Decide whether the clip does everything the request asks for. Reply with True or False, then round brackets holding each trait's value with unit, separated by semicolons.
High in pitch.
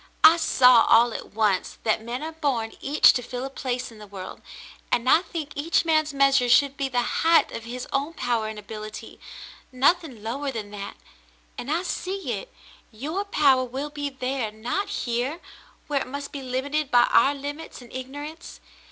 True (265 Hz)